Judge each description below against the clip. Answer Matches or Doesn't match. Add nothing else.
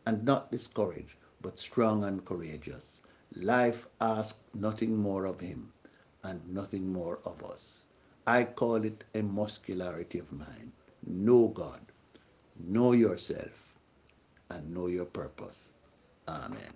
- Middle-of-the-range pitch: Doesn't match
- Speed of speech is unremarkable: Doesn't match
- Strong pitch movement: Doesn't match